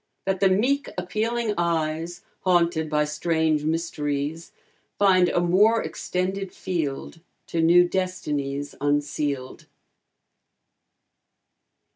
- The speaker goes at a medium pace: No, slow, 90 wpm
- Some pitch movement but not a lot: Yes, average, 3.6 semitones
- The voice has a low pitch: No, medium, 170 Hz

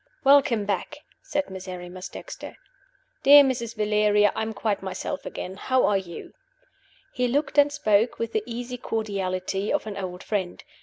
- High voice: Yes, high, 210 Hz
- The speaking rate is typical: Yes, average, 155 wpm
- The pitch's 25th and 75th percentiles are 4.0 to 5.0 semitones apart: Yes, average, 4.3 semitones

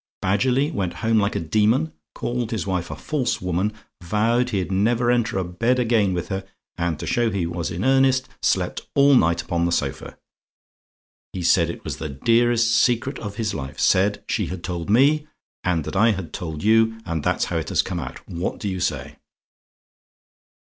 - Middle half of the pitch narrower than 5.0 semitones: No, wide, 5.5 semitones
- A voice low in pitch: Yes, low, 100 Hz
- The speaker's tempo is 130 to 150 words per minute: No, average, 190 wpm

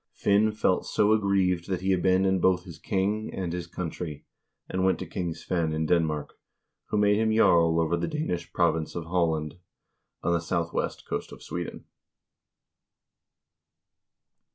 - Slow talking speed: No, average, 150 wpm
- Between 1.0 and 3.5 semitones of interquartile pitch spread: Yes, narrow, 2.6 semitones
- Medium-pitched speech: No, very low, 90 Hz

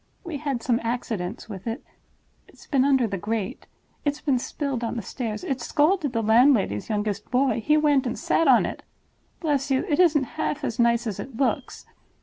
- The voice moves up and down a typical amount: Yes, average, 4.1 semitones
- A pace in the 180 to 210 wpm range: Yes, average, 185 wpm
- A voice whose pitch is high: Yes, very high, 250 Hz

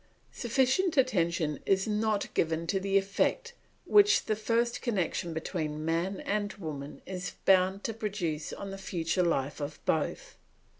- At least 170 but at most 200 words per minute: No, average, 145 wpm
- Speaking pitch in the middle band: No, high, 195 Hz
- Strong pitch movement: No, average, 4.7 semitones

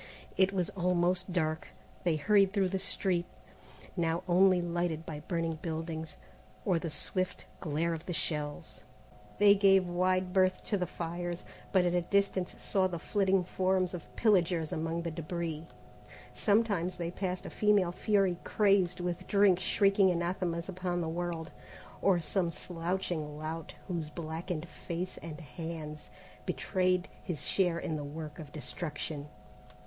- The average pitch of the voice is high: No, medium, 175 Hz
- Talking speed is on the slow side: No, average, 145 wpm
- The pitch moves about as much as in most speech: No, narrow, 2.3 semitones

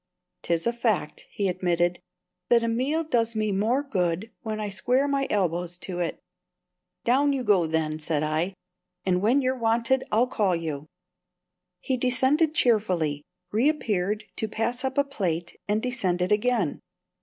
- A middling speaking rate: Yes, average, 155 wpm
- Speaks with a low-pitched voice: No, high, 215 Hz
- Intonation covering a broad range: Yes, wide, 5.9 semitones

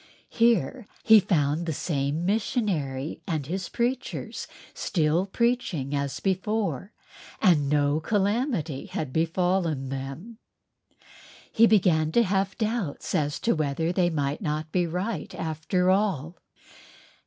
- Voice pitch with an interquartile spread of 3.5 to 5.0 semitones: No, wide, 5.5 semitones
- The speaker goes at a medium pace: No, slow, 115 wpm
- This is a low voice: No, medium, 175 Hz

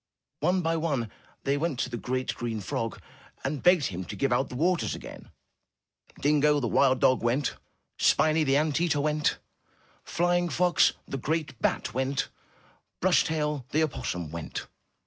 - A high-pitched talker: No, medium, 145 Hz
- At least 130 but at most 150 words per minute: No, average, 160 wpm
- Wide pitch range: No, average, 4.0 semitones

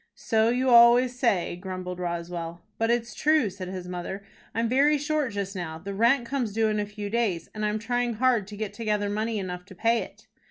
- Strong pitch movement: No, average, 4.2 semitones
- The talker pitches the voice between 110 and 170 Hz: No, high, 215 Hz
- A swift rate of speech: Yes, fast, 215 wpm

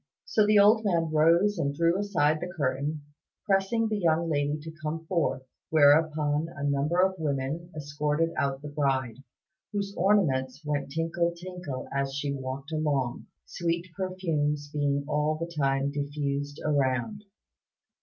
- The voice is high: No, medium, 150 Hz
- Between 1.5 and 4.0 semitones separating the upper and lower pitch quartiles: Yes, average, 3.3 semitones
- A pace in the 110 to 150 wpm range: Yes, average, 145 wpm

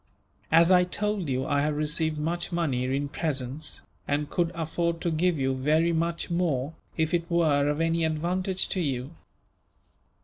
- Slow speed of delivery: No, average, 165 wpm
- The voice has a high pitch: No, medium, 160 Hz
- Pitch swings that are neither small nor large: Yes, average, 3.0 semitones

